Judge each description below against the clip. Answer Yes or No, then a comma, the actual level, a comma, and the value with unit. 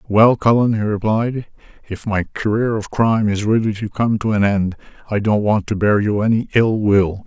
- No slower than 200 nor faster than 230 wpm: Yes, fast, 205 wpm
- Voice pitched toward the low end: Yes, low, 105 Hz